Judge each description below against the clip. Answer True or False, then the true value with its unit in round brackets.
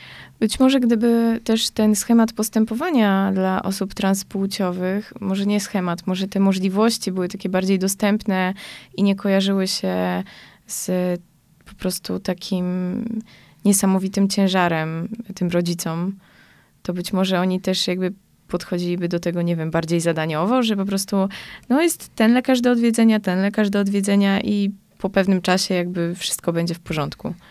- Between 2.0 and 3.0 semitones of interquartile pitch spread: True (2.6 semitones)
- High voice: True (195 Hz)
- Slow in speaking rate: False (145 wpm)